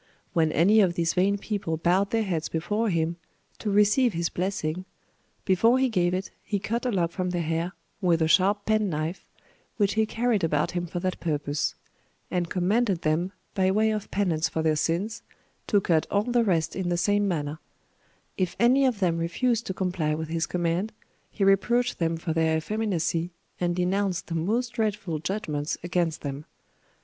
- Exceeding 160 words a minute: Yes, average, 180 wpm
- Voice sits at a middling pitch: Yes, medium, 180 Hz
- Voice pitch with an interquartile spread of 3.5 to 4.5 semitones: Yes, average, 4.0 semitones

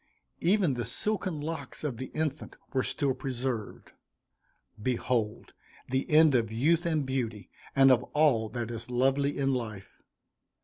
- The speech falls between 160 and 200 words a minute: No, average, 140 wpm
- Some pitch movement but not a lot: Yes, average, 4.1 semitones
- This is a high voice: No, low, 130 Hz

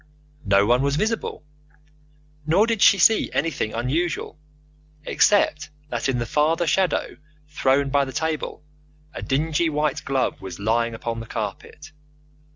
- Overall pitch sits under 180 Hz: Yes, medium, 140 Hz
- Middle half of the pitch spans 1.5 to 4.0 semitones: No, wide, 5.6 semitones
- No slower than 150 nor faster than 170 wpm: No, average, 140 wpm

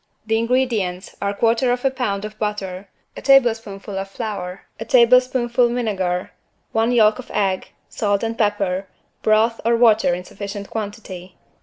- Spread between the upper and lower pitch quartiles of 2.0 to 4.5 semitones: Yes, average, 3.1 semitones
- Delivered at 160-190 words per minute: No, average, 140 wpm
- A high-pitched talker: Yes, high, 215 Hz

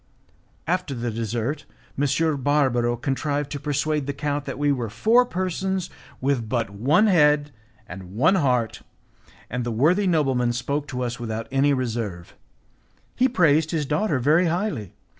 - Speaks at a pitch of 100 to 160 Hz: Yes, medium, 140 Hz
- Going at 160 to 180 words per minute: No, average, 150 wpm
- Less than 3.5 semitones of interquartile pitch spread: No, average, 4.6 semitones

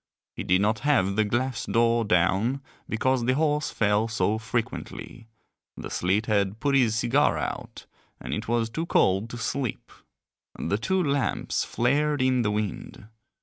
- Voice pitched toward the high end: No, low, 115 Hz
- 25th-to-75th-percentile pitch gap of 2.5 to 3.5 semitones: No, average, 4.0 semitones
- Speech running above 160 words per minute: No, average, 155 wpm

